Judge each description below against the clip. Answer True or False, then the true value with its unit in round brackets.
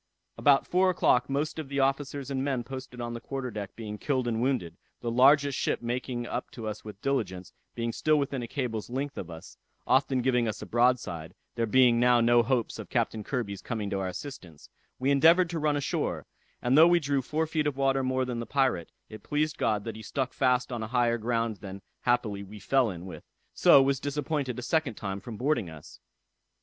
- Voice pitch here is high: False (125 Hz)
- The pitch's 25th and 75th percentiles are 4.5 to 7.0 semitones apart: False (3.8 semitones)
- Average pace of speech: False (215 wpm)